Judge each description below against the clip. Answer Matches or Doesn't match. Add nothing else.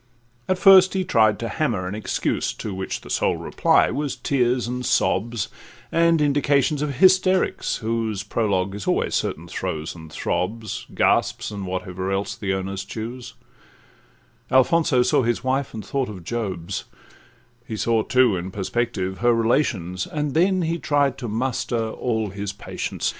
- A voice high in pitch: Doesn't match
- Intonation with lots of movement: Matches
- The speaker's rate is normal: Matches